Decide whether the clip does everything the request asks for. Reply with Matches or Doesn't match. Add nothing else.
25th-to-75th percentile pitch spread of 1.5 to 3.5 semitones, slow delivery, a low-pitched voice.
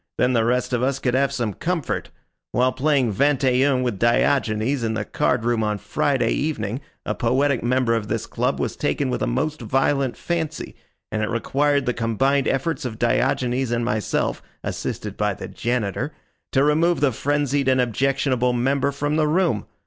Doesn't match